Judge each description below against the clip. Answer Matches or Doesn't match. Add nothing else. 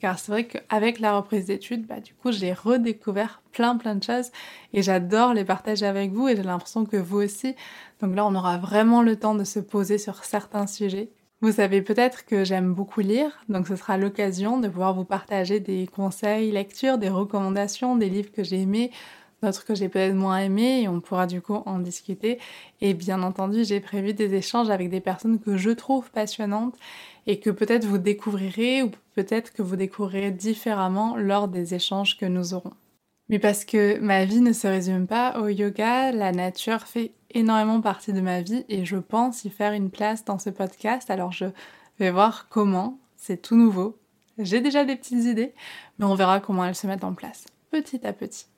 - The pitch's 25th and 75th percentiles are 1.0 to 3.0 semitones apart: Matches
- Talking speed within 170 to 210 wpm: Matches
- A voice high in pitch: Matches